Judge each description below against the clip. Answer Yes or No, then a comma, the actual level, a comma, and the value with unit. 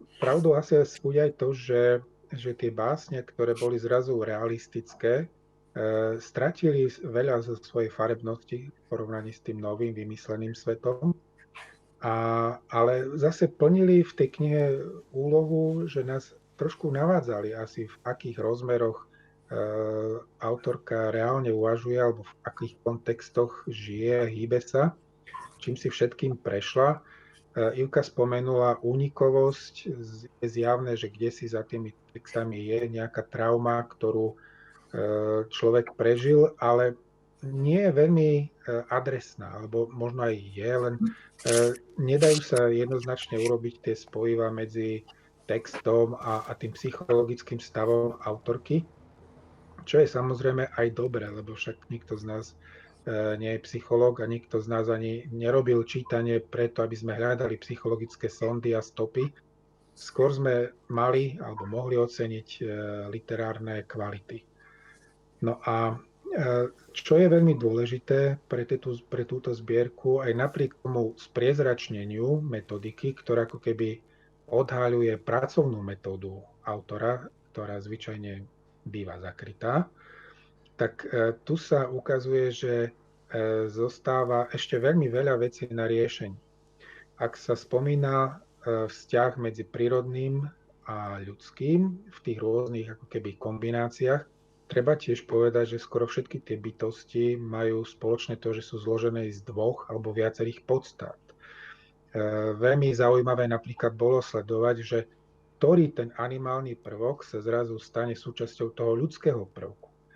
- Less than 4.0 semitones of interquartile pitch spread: Yes, narrow, 2.5 semitones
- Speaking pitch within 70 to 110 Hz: No, low, 120 Hz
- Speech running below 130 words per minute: Yes, average, 120 wpm